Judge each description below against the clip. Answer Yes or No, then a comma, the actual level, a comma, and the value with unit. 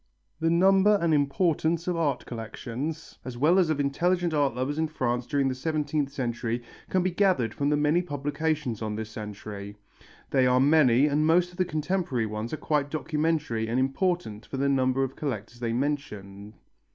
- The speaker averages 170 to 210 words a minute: Yes, average, 180 wpm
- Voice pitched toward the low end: No, medium, 145 Hz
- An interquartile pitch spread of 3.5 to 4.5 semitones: No, average, 4.9 semitones